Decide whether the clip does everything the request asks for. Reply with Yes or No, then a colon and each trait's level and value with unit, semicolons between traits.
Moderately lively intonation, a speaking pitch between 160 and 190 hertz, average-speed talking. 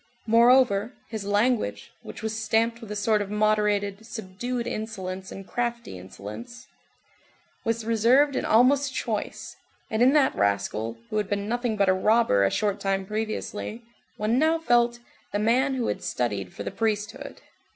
No: average, 3.2 semitones; high, 215 Hz; average, 160 wpm